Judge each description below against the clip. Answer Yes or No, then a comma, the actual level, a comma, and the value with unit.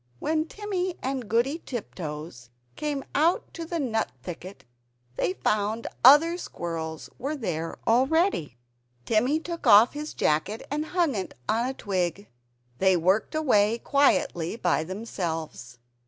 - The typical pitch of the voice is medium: No, high, 225 Hz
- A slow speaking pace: Yes, slow, 125 wpm